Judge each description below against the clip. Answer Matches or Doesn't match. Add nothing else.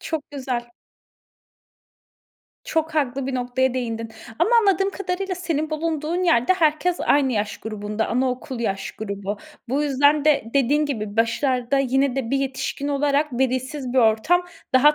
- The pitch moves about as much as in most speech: Matches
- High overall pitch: Matches